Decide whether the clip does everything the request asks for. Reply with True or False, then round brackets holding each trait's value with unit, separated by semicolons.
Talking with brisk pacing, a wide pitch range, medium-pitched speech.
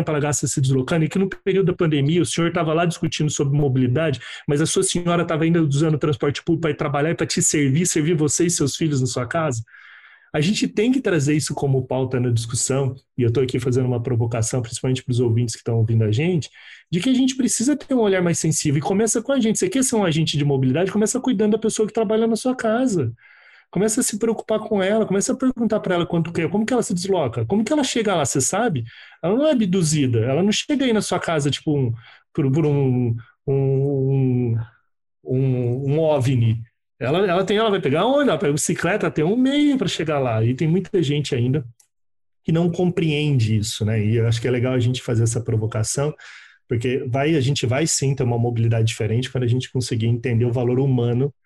True (230 wpm; 6.9 semitones; 150 Hz)